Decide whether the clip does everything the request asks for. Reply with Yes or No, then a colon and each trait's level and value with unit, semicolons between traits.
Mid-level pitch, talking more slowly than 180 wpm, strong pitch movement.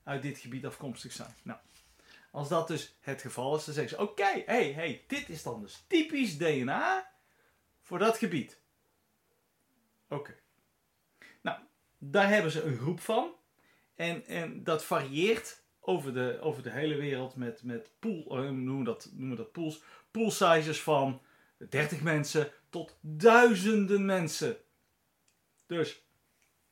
Yes: medium, 155 Hz; average, 145 wpm; wide, 6.6 semitones